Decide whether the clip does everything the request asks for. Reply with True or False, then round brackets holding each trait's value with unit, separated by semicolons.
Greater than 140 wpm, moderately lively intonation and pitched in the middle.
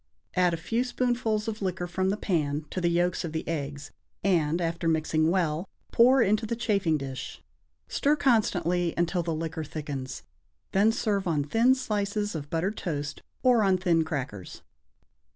True (170 wpm; 4.9 semitones; 175 Hz)